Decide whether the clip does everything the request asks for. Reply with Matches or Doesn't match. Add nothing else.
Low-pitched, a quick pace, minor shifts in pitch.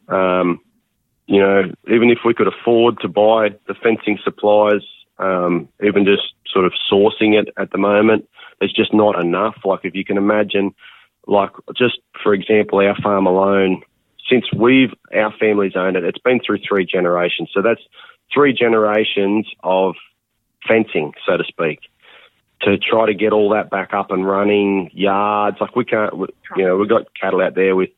Doesn't match